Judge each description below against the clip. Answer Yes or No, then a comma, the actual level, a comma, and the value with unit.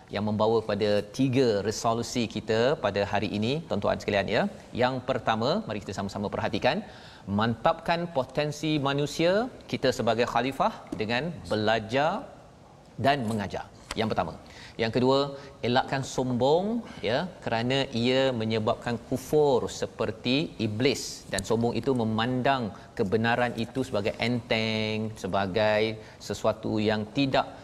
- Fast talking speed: No, average, 115 wpm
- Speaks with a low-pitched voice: Yes, low, 120 Hz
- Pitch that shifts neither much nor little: Yes, average, 3.8 semitones